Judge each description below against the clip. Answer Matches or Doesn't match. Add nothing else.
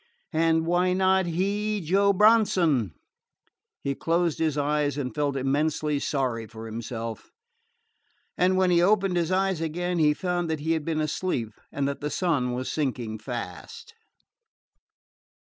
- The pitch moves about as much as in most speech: Matches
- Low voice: Doesn't match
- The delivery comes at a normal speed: Matches